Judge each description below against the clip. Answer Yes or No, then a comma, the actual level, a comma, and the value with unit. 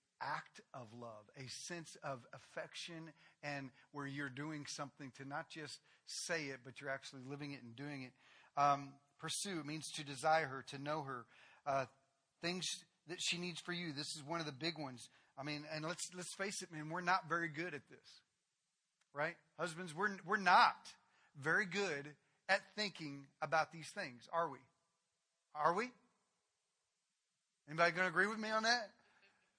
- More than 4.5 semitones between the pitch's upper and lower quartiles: No, average, 3.9 semitones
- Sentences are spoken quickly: No, average, 175 wpm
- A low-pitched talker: No, medium, 155 Hz